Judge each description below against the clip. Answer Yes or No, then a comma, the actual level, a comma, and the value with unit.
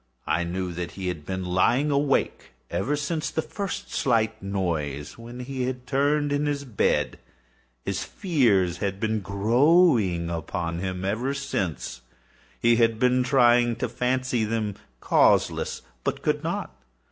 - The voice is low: Yes, low, 115 Hz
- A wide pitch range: Yes, wide, 6.2 semitones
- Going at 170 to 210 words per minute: No, average, 145 wpm